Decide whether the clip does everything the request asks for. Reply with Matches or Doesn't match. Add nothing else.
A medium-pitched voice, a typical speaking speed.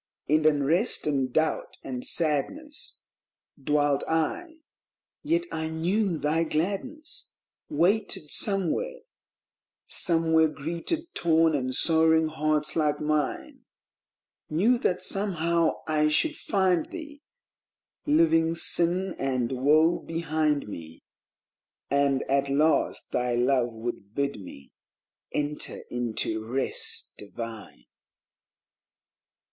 Doesn't match